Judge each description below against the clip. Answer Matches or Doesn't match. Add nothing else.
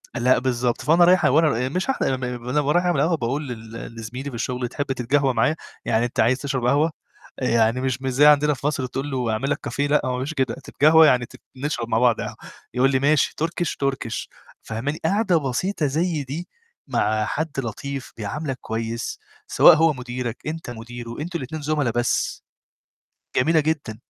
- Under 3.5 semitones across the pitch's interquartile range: Doesn't match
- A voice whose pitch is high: Doesn't match